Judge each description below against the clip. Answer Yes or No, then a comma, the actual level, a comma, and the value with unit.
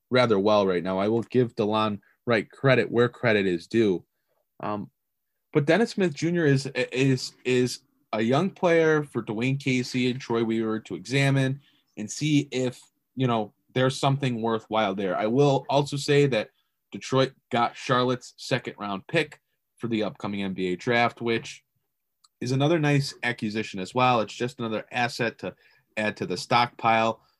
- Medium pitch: No, low, 125 Hz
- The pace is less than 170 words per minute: Yes, average, 160 wpm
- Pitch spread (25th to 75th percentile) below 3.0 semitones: No, average, 3.6 semitones